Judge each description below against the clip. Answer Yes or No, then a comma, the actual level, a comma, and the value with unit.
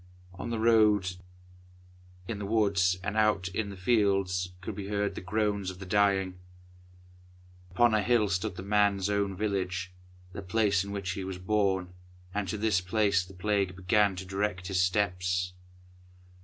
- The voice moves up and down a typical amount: No, narrow, 2.2 semitones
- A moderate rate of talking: Yes, average, 170 wpm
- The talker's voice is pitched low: Yes, low, 100 Hz